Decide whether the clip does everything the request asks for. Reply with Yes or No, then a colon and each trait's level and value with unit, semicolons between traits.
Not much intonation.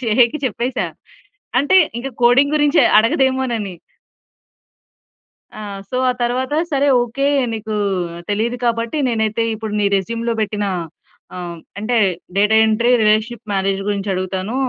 No: average, 3.1 semitones